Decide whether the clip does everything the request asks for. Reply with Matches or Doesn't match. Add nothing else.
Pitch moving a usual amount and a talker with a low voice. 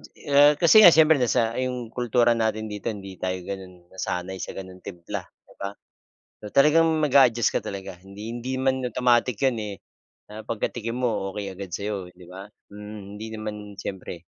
Matches